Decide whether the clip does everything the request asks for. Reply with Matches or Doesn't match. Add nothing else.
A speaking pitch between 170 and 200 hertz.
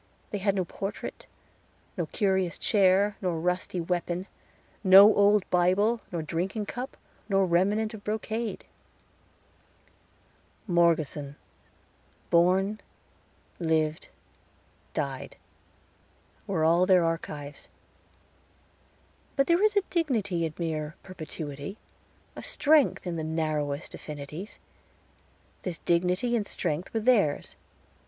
Matches